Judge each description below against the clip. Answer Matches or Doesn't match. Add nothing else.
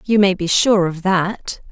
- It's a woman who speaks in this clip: Matches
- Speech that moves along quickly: Matches